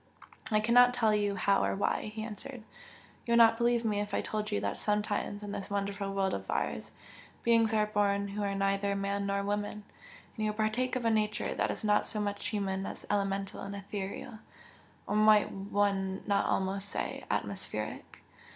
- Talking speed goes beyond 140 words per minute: Yes, average, 190 wpm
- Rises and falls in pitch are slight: Yes, narrow, 1.5 semitones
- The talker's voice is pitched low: No, high, 205 Hz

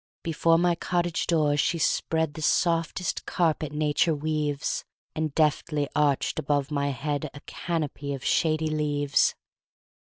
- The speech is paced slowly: Yes, slow, 115 wpm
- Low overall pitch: No, medium, 155 Hz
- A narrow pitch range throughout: Yes, narrow, 2.1 semitones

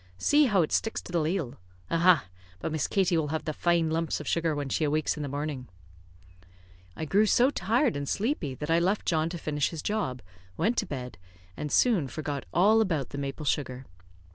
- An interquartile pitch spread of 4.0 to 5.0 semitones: Yes, average, 4.6 semitones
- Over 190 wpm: Yes, fast, 205 wpm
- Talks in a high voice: No, medium, 160 Hz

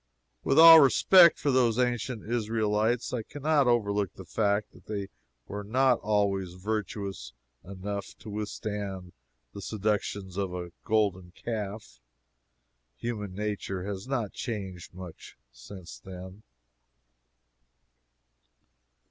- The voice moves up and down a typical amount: Yes, average, 3.1 semitones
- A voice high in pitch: No, low, 105 Hz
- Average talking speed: No, slow, 115 wpm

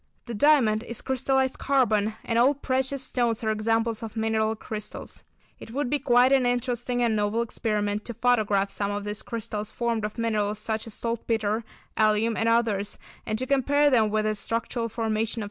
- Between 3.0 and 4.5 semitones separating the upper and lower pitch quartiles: No, narrow, 2.4 semitones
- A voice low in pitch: No, high, 225 Hz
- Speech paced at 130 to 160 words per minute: No, average, 190 wpm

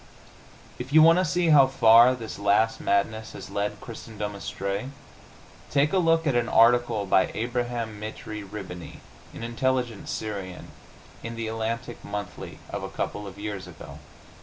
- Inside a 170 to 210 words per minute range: No, average, 155 wpm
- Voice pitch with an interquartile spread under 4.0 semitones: Yes, average, 3.2 semitones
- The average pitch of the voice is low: Yes, low, 110 Hz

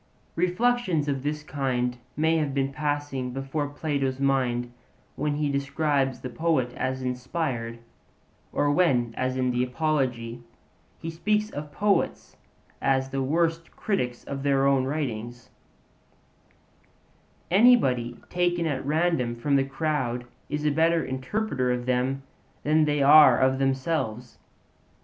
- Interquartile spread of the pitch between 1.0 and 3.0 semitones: No, average, 3.5 semitones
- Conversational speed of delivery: No, slow, 130 wpm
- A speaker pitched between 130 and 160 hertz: Yes, medium, 140 Hz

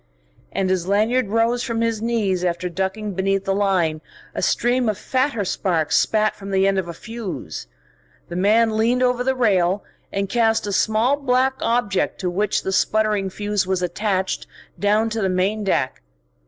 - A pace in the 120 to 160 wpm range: No, average, 175 wpm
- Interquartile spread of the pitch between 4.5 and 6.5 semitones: No, average, 3.2 semitones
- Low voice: No, high, 205 Hz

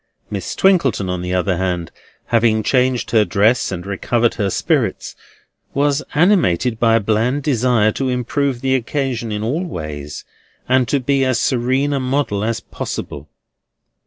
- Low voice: Yes, low, 120 Hz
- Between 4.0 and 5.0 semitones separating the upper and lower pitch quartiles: Yes, average, 4.6 semitones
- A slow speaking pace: No, average, 155 wpm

